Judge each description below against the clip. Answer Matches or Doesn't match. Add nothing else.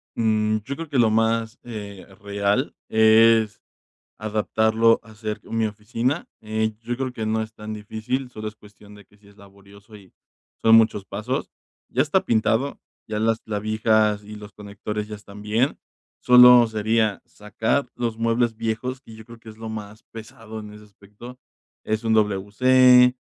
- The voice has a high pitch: Doesn't match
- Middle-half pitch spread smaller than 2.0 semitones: Matches